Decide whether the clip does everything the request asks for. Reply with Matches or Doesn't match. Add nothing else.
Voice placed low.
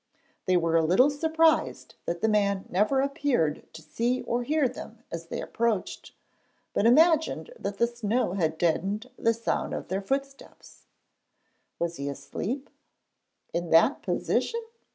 Doesn't match